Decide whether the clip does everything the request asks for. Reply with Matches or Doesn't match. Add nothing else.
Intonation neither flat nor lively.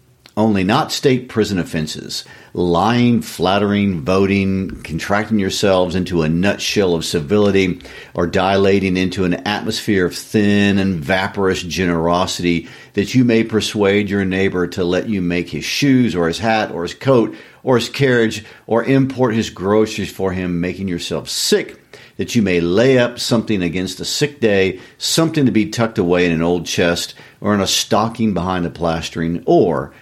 Matches